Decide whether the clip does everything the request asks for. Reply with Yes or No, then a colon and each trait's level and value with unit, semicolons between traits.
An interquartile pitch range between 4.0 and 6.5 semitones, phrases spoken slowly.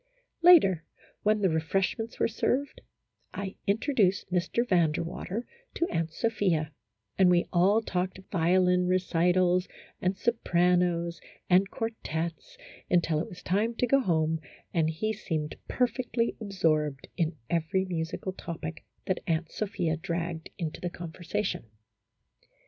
No: average, 3.6 semitones; slow, 130 wpm